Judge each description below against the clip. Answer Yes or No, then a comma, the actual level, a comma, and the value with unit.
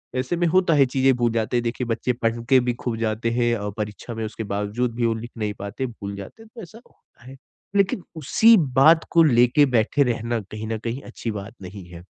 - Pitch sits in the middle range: No, low, 120 Hz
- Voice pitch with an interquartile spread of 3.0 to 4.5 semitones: Yes, average, 3.5 semitones